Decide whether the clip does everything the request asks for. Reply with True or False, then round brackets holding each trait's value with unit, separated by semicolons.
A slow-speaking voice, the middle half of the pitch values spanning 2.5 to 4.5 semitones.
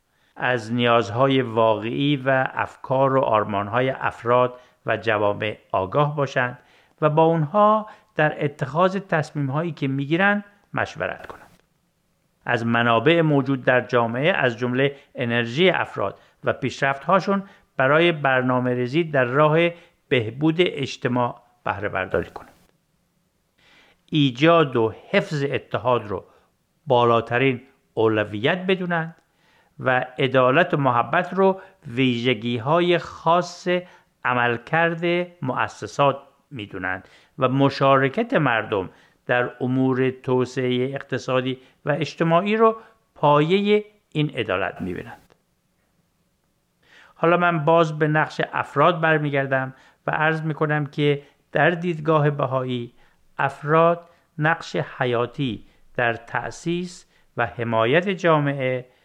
False (100 wpm; 5.0 semitones)